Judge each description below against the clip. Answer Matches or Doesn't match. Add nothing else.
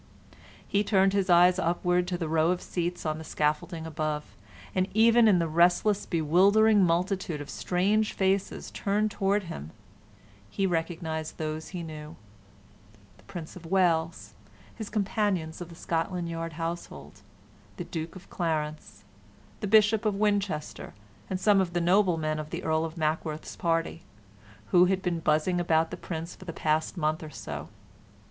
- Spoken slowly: Doesn't match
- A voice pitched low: Doesn't match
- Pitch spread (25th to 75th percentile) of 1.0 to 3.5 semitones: Matches